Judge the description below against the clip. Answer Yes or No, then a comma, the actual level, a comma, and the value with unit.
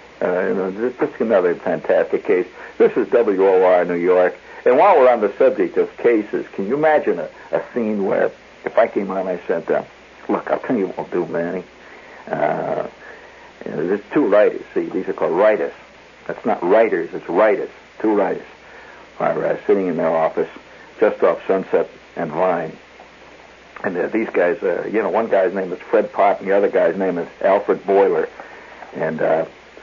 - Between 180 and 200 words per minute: Yes, average, 195 wpm